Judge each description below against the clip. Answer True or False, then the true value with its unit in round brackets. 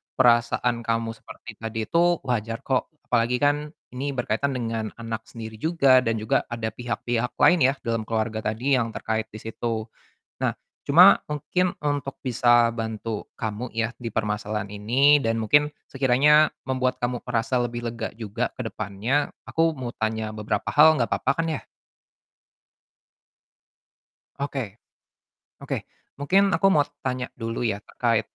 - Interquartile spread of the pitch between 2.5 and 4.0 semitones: True (3.2 semitones)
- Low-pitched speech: True (120 Hz)